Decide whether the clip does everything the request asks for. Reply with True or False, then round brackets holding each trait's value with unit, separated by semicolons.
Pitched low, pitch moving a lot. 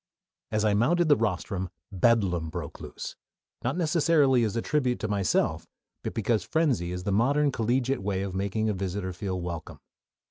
True (110 Hz; 5.7 semitones)